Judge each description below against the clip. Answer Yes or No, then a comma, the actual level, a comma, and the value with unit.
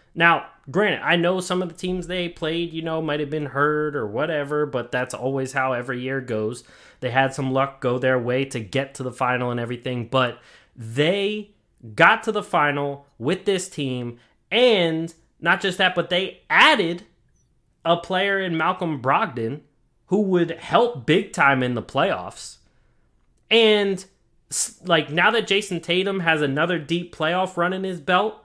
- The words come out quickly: No, average, 175 wpm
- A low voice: No, medium, 160 Hz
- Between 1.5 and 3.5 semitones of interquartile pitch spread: No, wide, 5.5 semitones